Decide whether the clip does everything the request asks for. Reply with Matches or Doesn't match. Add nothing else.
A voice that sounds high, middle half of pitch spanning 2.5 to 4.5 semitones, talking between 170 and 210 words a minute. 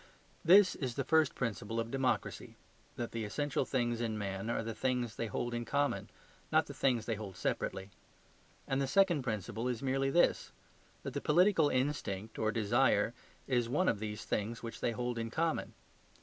Doesn't match